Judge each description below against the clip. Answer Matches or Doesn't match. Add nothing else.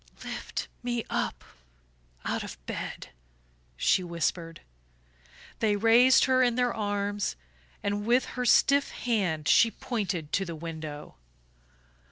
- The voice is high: Matches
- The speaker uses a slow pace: Matches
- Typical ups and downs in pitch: Doesn't match